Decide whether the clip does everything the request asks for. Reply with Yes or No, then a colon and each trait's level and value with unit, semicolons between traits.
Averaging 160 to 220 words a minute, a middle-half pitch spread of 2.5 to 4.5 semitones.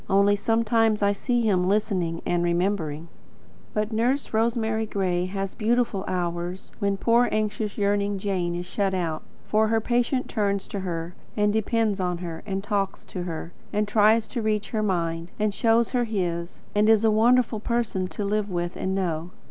Yes: average, 175 wpm; average, 3.4 semitones